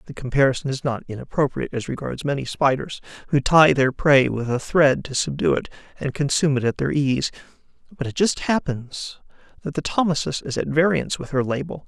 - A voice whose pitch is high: No, medium, 140 Hz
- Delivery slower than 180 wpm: No, average, 190 wpm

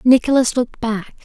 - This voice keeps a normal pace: Yes, average, 145 wpm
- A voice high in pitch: Yes, high, 240 Hz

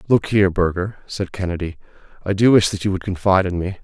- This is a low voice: Yes, very low, 95 Hz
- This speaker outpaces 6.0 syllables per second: Yes, 6.5 syllables/s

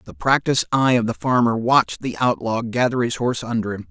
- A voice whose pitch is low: Yes, low, 115 Hz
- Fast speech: Yes, fast, 215 wpm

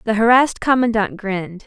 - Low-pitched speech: No, high, 220 Hz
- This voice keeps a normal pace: Yes, average, 145 wpm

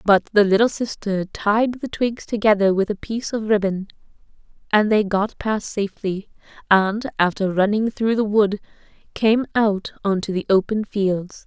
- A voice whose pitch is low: No, high, 205 Hz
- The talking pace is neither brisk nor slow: Yes, average, 160 wpm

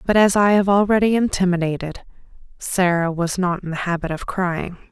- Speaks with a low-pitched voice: No, medium, 185 Hz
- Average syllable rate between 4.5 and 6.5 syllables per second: Yes, 5.0 syllables/s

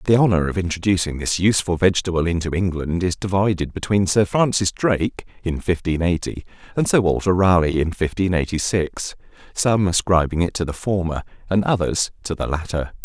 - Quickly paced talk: No, average, 170 wpm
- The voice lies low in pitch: Yes, very low, 90 Hz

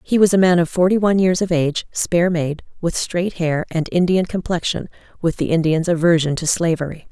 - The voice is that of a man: No, female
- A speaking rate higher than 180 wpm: Yes, average, 200 wpm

